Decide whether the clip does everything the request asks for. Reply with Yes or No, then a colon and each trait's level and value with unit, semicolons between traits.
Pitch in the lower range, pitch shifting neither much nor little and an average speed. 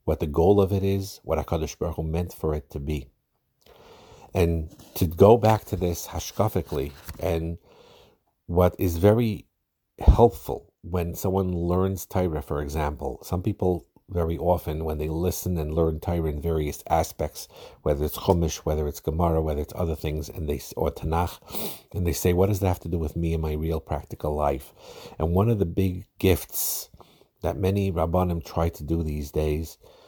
Yes: very low, 85 Hz; average, 3.0 semitones; average, 180 wpm